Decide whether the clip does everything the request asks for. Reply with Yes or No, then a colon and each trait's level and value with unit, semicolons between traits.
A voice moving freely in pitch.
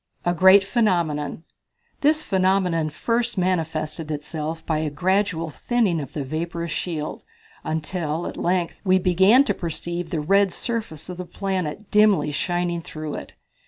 No: average, 3.5 semitones